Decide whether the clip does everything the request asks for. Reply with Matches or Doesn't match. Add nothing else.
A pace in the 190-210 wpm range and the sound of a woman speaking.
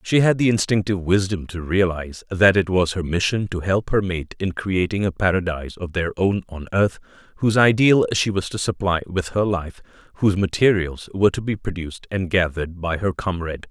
Doesn't match